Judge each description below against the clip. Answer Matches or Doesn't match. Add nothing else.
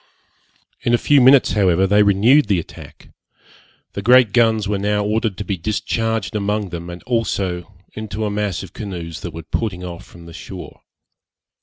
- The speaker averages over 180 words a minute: Doesn't match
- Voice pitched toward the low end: Matches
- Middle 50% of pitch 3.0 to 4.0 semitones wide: Matches